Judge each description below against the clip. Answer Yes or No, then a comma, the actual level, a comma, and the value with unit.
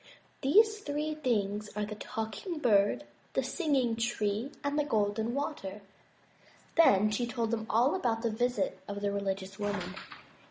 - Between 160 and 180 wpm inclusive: No, average, 150 wpm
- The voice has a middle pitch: No, high, 225 Hz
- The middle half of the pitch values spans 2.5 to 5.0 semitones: No, wide, 5.5 semitones